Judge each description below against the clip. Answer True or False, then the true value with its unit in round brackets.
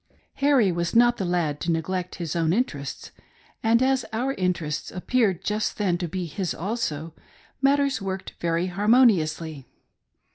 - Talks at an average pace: True (145 wpm)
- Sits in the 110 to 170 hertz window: False (185 Hz)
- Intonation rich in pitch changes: True (5.7 semitones)